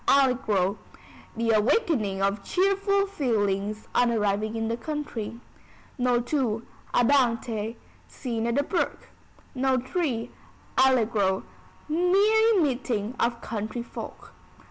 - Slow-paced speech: Yes, slow, 105 wpm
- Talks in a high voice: Yes, high, 240 Hz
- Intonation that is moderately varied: Yes, average, 4.8 semitones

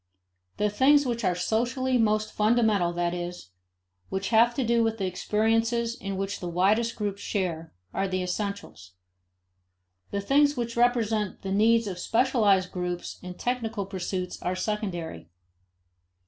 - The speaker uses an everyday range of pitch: Yes, average, 4.0 semitones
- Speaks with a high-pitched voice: Yes, high, 210 Hz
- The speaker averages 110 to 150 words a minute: Yes, average, 145 wpm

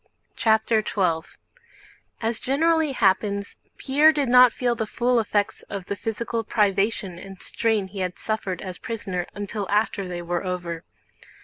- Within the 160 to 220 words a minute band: No, average, 145 wpm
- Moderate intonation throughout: Yes, average, 3.6 semitones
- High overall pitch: Yes, high, 210 Hz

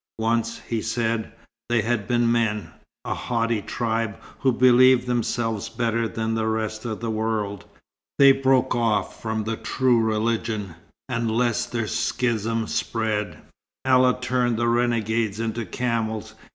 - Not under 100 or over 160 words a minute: Yes, average, 140 wpm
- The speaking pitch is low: Yes, low, 115 Hz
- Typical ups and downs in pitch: No, narrow, 1.5 semitones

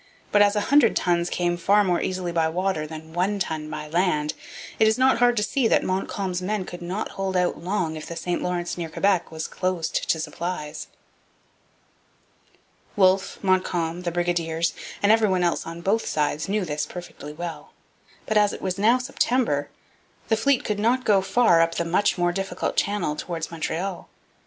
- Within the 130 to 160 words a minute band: No, average, 185 wpm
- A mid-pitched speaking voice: Yes, medium, 180 Hz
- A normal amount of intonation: Yes, average, 3.4 semitones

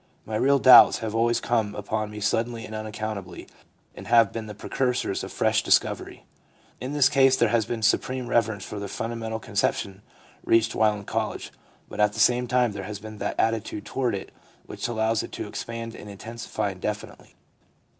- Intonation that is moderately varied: No, narrow, 2.1 semitones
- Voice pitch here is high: No, low, 110 Hz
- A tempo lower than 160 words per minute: No, average, 190 wpm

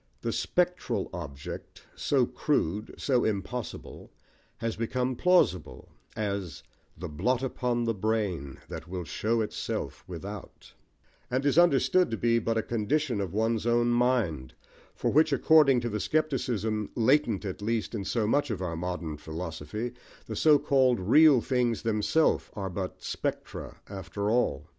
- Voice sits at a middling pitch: No, low, 115 Hz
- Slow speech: No, average, 145 wpm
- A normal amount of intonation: Yes, average, 4.9 semitones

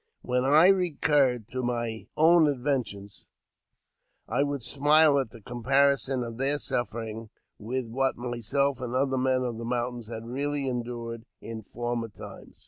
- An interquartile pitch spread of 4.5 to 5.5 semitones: No, average, 3.1 semitones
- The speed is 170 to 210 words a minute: No, average, 145 wpm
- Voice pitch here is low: Yes, low, 125 Hz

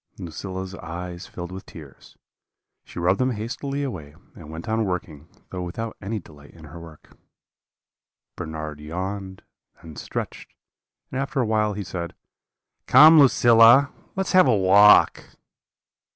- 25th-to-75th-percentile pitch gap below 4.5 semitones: No, average, 5.3 semitones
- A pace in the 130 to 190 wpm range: Yes, average, 140 wpm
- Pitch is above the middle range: No, very low, 95 Hz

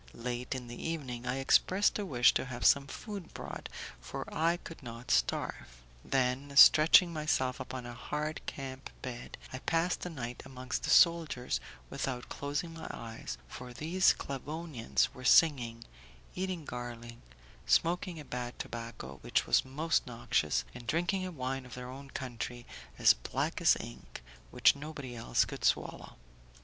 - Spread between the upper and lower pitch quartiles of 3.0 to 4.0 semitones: No, average, 4.5 semitones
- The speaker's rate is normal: Yes, average, 155 wpm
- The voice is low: Yes, low, 130 Hz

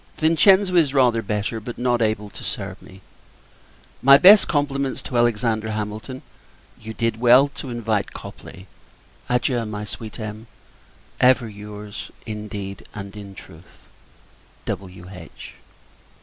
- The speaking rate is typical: No, slow, 125 wpm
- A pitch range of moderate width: Yes, average, 3.4 semitones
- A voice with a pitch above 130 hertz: No, low, 110 Hz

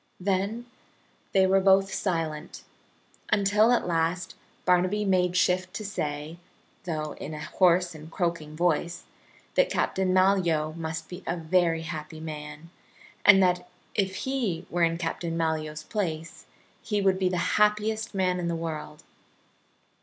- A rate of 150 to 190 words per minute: No, average, 140 wpm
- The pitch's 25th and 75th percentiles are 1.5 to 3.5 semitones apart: Yes, average, 2.9 semitones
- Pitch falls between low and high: Yes, medium, 180 Hz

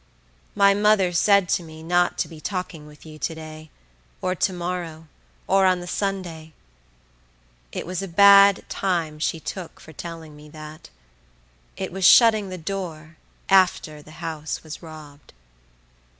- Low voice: No, medium, 170 Hz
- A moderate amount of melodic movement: Yes, average, 3.3 semitones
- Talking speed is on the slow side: No, average, 150 wpm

